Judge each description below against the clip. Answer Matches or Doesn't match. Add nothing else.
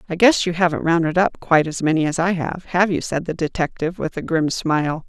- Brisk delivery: Matches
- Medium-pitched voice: Matches